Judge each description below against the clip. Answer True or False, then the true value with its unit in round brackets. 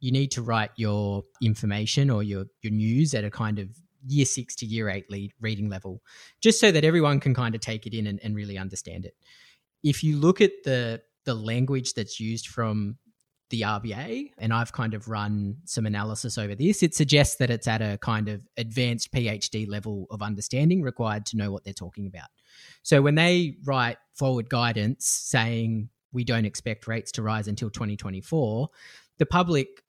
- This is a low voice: True (115 Hz)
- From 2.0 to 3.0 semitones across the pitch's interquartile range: False (4.2 semitones)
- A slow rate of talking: False (190 wpm)